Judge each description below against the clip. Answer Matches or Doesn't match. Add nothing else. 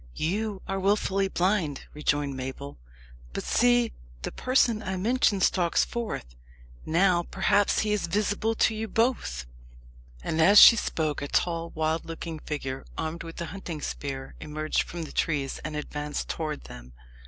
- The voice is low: Doesn't match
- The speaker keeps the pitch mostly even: Doesn't match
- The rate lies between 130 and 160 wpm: Matches